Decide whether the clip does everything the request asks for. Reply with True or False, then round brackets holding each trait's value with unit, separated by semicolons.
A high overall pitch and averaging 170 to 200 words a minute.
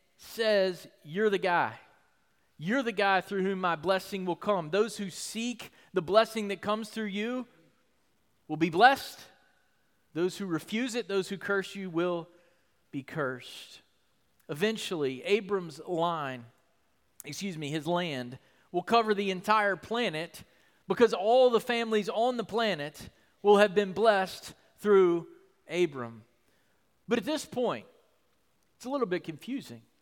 False (195 Hz; 140 wpm)